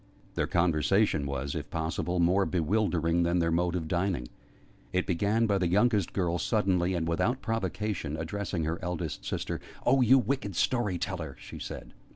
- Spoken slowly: No, average, 165 wpm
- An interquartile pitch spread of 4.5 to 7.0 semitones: No, average, 3.7 semitones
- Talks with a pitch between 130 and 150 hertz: No, very low, 90 Hz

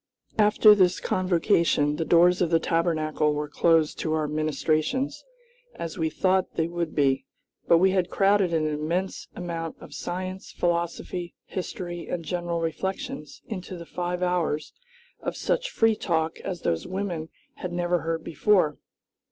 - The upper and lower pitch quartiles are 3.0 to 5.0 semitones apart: No, narrow, 2.6 semitones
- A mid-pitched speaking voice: Yes, medium, 170 Hz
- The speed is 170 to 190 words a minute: No, average, 150 wpm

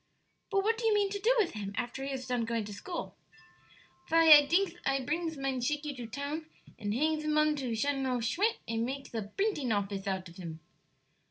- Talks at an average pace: No, fast, 210 wpm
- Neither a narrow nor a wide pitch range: No, wide, 5.9 semitones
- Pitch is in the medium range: No, very high, 275 Hz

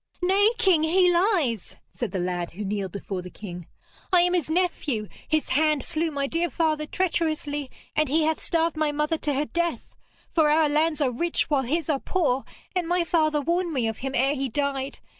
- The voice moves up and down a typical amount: Yes, average, 4.0 semitones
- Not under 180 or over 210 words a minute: Yes, average, 200 wpm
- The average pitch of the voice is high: Yes, very high, 305 Hz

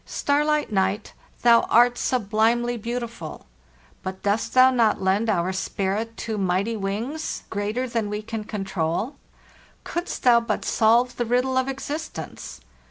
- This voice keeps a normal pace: Yes, average, 145 wpm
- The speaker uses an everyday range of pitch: Yes, average, 3.4 semitones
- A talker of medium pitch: No, high, 225 Hz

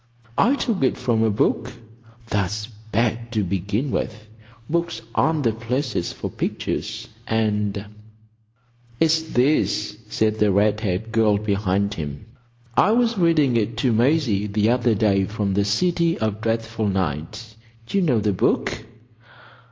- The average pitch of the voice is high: No, low, 110 Hz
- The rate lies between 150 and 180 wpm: No, average, 140 wpm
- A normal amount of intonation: Yes, average, 3.7 semitones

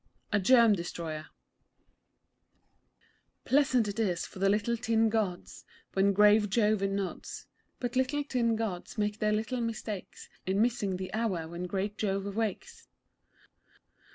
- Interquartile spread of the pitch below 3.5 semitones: Yes, average, 2.9 semitones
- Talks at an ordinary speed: No, slow, 130 wpm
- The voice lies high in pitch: Yes, high, 210 Hz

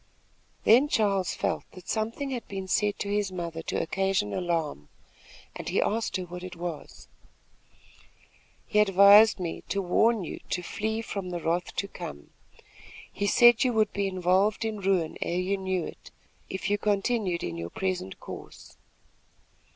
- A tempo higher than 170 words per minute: No, average, 160 wpm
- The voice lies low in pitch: No, high, 195 Hz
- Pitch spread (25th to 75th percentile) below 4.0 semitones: Yes, average, 2.9 semitones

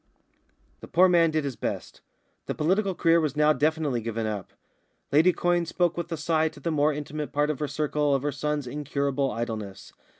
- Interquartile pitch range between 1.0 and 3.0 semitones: Yes, narrow, 2.6 semitones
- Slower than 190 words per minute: No, average, 195 wpm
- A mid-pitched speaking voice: Yes, medium, 150 Hz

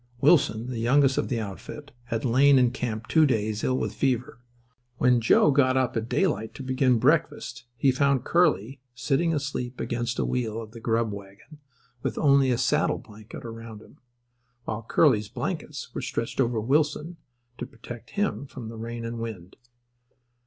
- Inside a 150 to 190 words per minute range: Yes, average, 170 wpm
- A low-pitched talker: Yes, low, 125 Hz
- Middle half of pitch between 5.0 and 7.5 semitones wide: No, average, 3.4 semitones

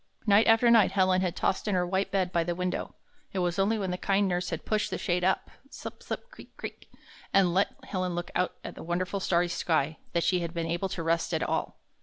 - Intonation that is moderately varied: No, narrow, 2.0 semitones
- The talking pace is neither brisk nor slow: No, fast, 245 wpm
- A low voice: No, medium, 185 Hz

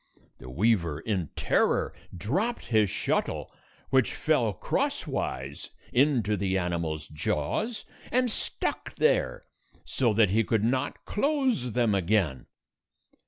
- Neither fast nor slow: No, slow, 115 wpm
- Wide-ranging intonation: Yes, wide, 8.5 semitones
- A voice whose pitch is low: Yes, low, 110 Hz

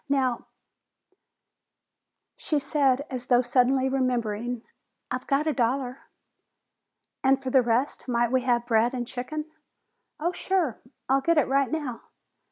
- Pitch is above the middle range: Yes, very high, 260 Hz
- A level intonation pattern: Yes, narrow, 2.2 semitones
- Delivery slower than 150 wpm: Yes, average, 140 wpm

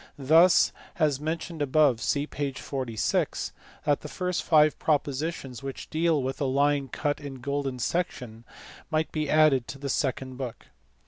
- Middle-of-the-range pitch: Yes, medium, 145 Hz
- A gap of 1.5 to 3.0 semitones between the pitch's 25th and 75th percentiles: Yes, average, 2.7 semitones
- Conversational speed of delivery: Yes, average, 145 wpm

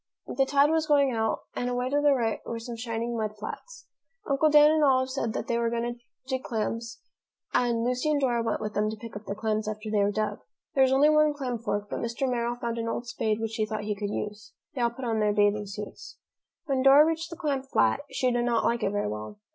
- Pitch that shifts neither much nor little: Yes, average, 3.7 semitones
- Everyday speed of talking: No, fast, 250 wpm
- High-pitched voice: Yes, high, 235 Hz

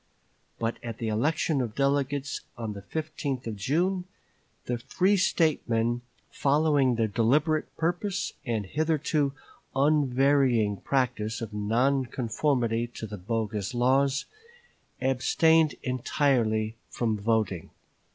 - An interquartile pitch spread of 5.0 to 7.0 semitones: No, average, 4.3 semitones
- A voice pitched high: No, low, 130 Hz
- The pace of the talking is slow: Yes, slow, 110 wpm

